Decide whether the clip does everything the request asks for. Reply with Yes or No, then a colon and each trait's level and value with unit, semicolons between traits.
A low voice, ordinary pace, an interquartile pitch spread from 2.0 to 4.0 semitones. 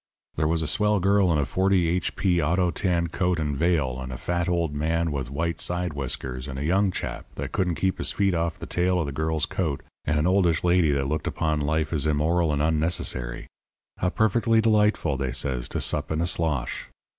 No: very low, 80 Hz; fast, 215 wpm; average, 3.5 semitones